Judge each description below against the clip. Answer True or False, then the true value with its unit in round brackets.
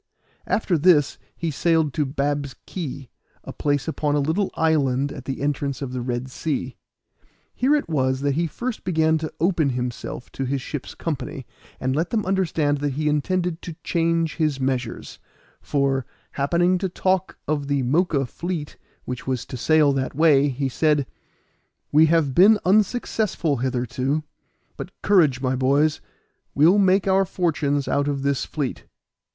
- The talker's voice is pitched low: False (145 Hz)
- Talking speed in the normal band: True (160 wpm)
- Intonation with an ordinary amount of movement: True (3.7 semitones)